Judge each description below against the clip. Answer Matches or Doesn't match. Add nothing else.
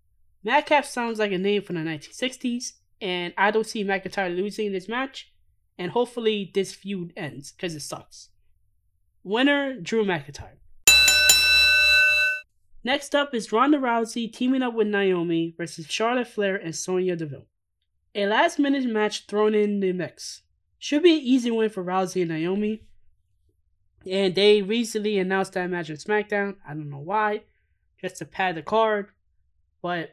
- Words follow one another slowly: Doesn't match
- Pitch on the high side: Matches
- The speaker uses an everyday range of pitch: Doesn't match